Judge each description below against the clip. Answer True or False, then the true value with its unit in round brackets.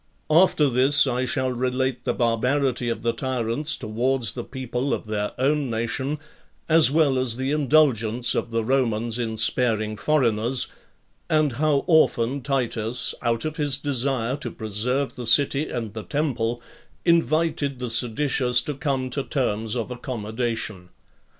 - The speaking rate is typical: True (150 wpm)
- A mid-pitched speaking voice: False (125 Hz)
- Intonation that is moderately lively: True (3.4 semitones)